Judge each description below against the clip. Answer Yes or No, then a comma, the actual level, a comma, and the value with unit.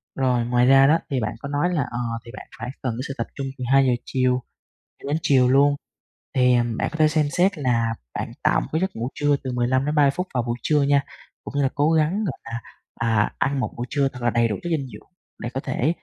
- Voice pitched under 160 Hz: Yes, low, 135 Hz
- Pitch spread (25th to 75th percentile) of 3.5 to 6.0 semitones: No, average, 3.1 semitones